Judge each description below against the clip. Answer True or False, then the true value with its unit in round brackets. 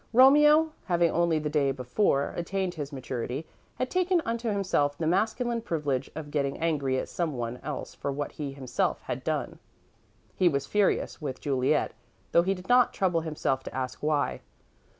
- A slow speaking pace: False (170 wpm)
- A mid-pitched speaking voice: True (155 Hz)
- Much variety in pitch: True (6.0 semitones)